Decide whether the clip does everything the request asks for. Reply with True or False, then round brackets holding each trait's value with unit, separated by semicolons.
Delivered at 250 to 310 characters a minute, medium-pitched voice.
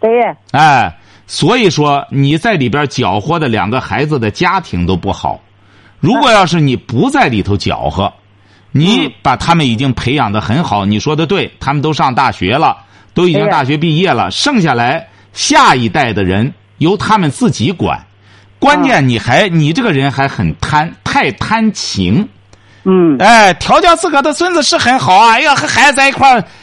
True (255 characters per minute; 145 Hz)